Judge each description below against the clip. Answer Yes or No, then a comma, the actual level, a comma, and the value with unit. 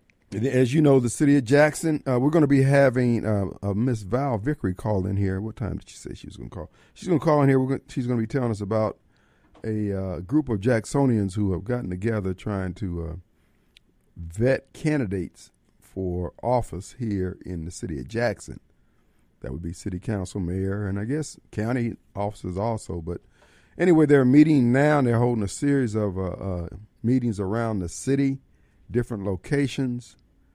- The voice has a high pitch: No, low, 110 Hz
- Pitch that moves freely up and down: Yes, wide, 5.7 semitones